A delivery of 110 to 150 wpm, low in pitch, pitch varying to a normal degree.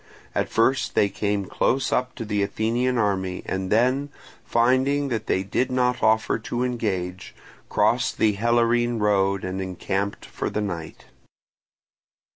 Yes: average, 140 wpm; low, 110 Hz; average, 4.0 semitones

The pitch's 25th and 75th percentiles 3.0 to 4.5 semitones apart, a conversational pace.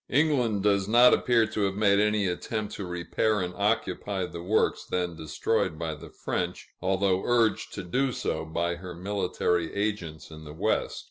Yes: average, 3.6 semitones; average, 175 wpm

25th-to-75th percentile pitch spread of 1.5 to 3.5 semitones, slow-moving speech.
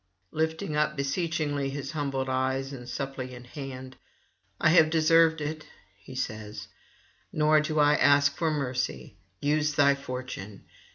Yes: average, 2.9 semitones; slow, 130 wpm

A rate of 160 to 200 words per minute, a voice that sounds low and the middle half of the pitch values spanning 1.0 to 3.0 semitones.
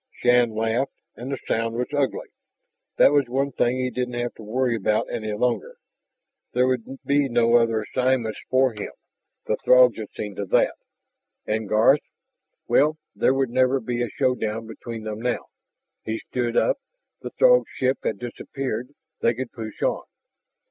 Yes: average, 165 wpm; low, 120 Hz; narrow, 2.6 semitones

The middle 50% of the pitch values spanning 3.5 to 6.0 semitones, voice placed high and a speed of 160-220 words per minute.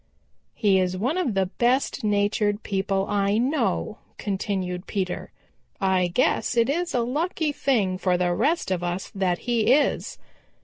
No: average, 5.0 semitones; high, 205 Hz; average, 150 wpm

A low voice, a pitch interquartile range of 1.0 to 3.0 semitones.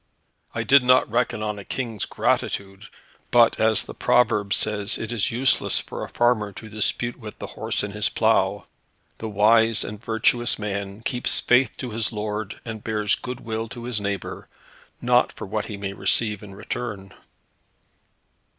Yes: low, 110 Hz; narrow, 2.4 semitones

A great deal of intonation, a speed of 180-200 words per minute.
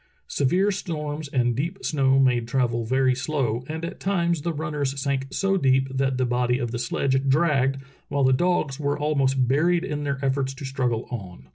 No: average, 2.9 semitones; average, 185 wpm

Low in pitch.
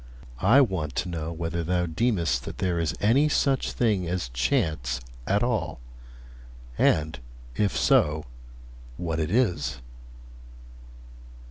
Yes: very low, 85 Hz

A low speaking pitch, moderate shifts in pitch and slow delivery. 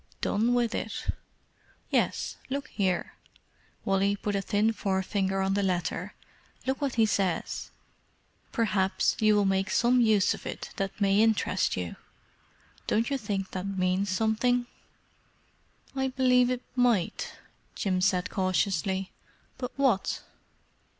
No: high, 205 Hz; average, 3.7 semitones; slow, 125 wpm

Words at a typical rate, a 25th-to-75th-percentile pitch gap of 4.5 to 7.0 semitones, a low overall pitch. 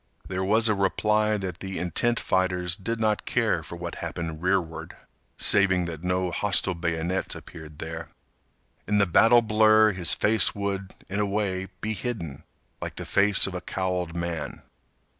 No: average, 160 wpm; average, 3.2 semitones; very low, 95 Hz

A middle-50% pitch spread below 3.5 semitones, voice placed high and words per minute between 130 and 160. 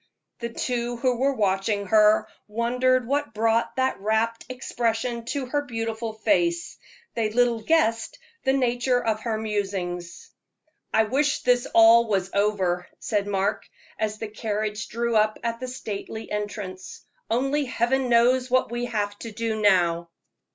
Yes: average, 2.8 semitones; high, 230 Hz; average, 145 wpm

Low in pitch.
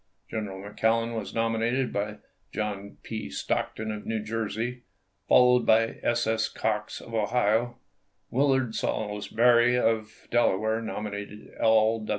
Yes: low, 110 Hz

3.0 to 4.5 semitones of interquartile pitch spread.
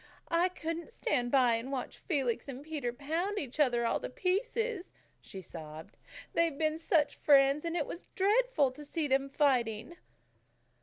No: average, 5.1 semitones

